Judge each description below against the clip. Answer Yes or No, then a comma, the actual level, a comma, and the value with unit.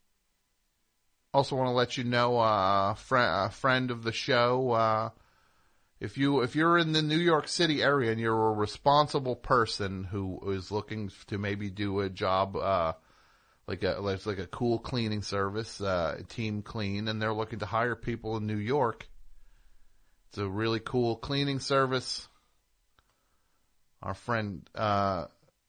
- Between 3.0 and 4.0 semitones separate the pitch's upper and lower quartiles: Yes, average, 3.7 semitones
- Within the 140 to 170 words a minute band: Yes, average, 155 wpm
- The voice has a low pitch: Yes, low, 110 Hz